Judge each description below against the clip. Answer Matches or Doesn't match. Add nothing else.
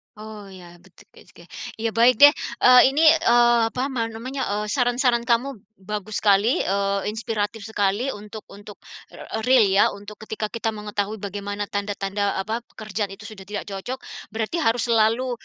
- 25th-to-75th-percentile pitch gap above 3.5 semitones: Doesn't match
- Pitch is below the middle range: Doesn't match